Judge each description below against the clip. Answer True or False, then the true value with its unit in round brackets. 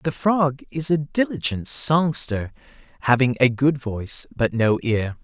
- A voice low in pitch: True (130 Hz)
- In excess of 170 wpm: False (150 wpm)